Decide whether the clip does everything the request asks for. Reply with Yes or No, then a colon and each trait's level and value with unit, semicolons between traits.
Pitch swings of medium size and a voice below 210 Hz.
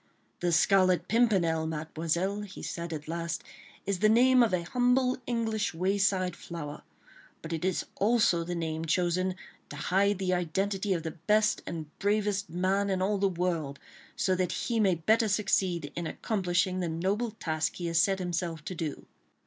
Yes: average, 3.3 semitones; medium, 185 Hz